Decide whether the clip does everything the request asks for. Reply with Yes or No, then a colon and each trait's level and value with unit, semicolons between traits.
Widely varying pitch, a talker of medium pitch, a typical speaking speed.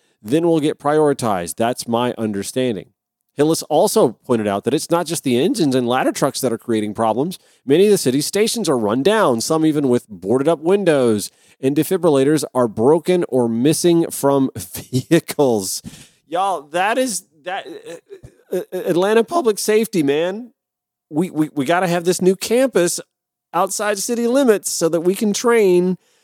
Yes: wide, 6.9 semitones; medium, 165 Hz; average, 165 wpm